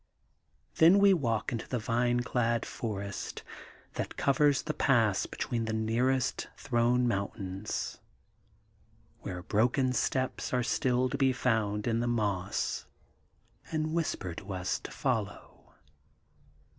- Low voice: Yes, low, 120 Hz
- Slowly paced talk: Yes, slow, 125 wpm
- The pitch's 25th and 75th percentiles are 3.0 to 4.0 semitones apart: Yes, average, 3.4 semitones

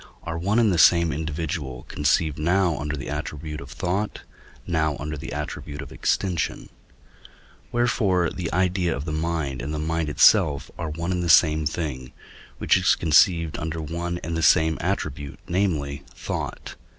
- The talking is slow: No, average, 160 wpm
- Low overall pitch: Yes, very low, 80 Hz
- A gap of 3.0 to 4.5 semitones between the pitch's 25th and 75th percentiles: No, narrow, 2.6 semitones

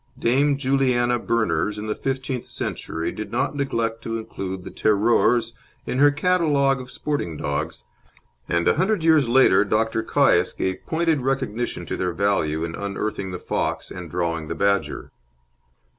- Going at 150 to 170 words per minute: Yes, average, 155 wpm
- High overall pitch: No, low, 115 Hz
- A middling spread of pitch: No, wide, 6.1 semitones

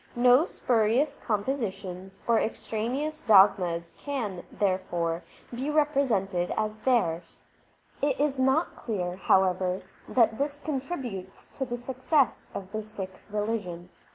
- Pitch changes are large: Yes, wide, 5.9 semitones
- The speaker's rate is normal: No, slow, 115 wpm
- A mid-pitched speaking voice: No, high, 220 Hz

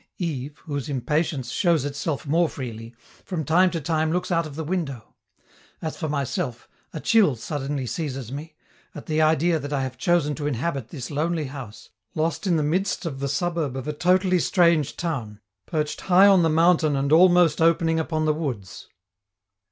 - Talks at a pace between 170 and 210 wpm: Yes, average, 180 wpm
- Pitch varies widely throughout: No, average, 3.3 semitones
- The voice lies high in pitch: No, medium, 155 Hz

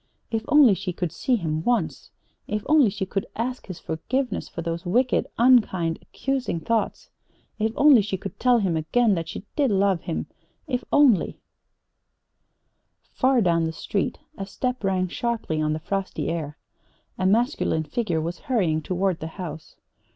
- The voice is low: No, high, 195 Hz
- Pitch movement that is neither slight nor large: No, wide, 6.4 semitones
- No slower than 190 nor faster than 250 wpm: No, average, 160 wpm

